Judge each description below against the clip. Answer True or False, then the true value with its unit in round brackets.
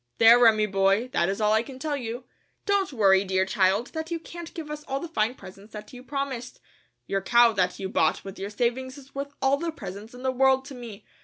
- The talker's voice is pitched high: True (240 Hz)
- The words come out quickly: True (235 wpm)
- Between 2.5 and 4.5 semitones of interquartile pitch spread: False (5.2 semitones)